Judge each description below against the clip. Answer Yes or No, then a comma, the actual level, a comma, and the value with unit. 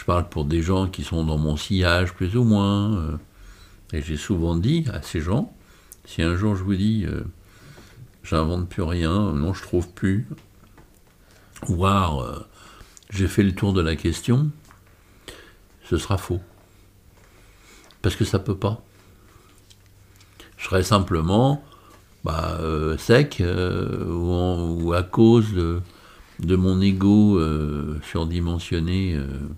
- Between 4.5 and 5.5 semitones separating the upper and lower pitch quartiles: No, average, 3.2 semitones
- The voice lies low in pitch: Yes, very low, 95 Hz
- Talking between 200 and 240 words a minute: No, slow, 145 wpm